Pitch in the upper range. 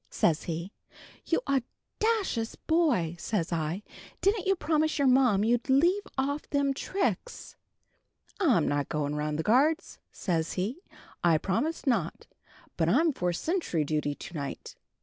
Yes: high, 240 Hz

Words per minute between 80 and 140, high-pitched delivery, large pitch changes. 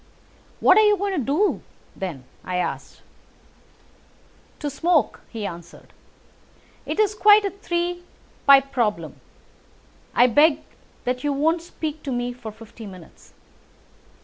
Yes: slow, 135 wpm; very high, 280 Hz; wide, 7.4 semitones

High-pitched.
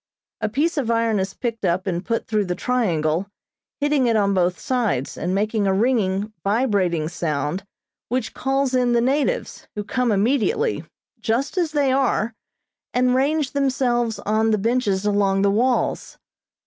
Yes: high, 225 Hz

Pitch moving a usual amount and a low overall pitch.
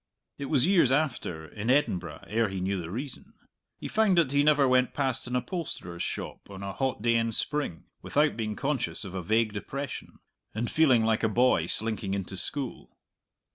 No: wide, 6.1 semitones; low, 120 Hz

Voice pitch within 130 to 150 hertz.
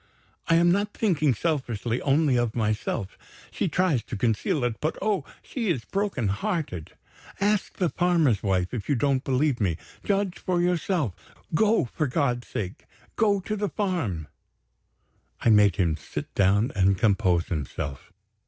Yes: low, 135 Hz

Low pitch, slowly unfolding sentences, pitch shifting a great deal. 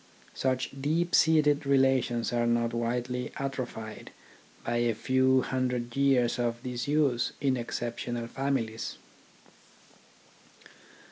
No: low, 125 Hz; slow, 95 wpm; narrow, 2.4 semitones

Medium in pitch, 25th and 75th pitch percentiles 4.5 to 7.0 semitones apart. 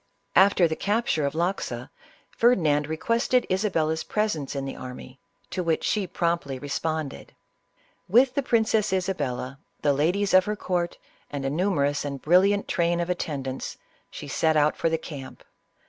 Yes: medium, 170 Hz; average, 5.1 semitones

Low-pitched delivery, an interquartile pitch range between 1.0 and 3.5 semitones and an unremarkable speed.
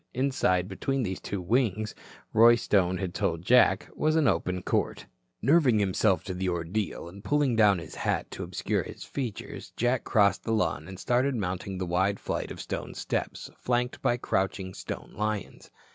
No: low, 100 Hz; average, 4.7 semitones; average, 175 wpm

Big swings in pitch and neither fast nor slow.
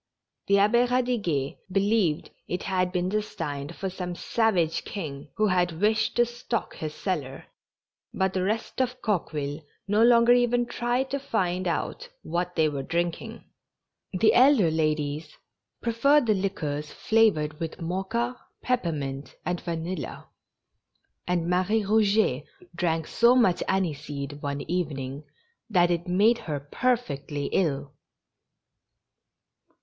No: wide, 6.3 semitones; slow, 125 wpm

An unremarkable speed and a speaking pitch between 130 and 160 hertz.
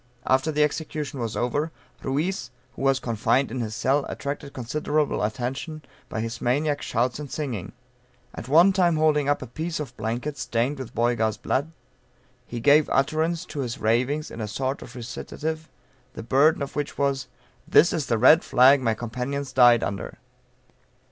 Yes: average, 170 wpm; low, 135 Hz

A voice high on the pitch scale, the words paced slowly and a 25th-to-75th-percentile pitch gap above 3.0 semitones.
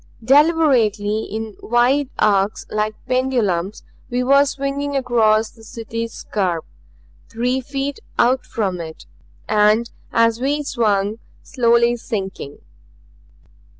Yes: high, 230 Hz; slow, 105 wpm; average, 3.6 semitones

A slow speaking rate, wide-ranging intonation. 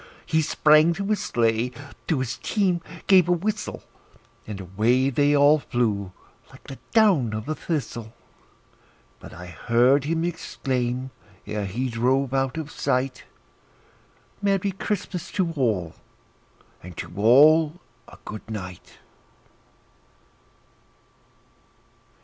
Yes: slow, 115 wpm; wide, 6.3 semitones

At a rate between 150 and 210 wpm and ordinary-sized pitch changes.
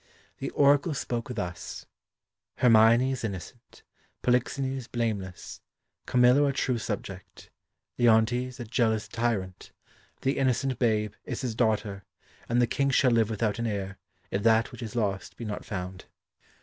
No: average, 140 wpm; average, 3.0 semitones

